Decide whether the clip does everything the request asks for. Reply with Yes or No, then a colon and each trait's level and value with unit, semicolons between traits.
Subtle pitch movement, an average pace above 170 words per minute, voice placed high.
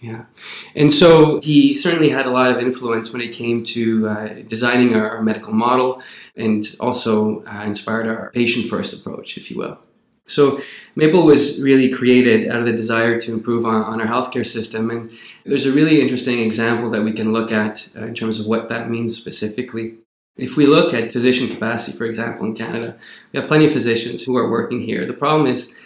No: narrow, 2.1 semitones; fast, 205 wpm; low, 115 Hz